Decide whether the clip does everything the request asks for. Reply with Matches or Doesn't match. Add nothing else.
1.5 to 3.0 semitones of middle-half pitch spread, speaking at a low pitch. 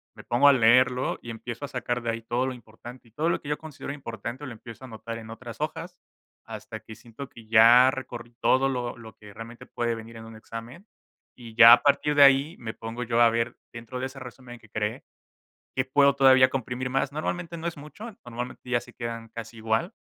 Matches